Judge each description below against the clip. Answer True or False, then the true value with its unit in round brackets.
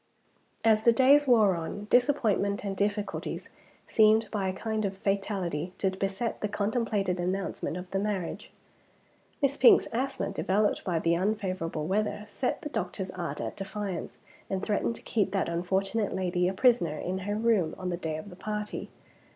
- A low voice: False (200 Hz)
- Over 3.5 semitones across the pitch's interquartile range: False (2.8 semitones)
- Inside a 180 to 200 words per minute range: False (165 wpm)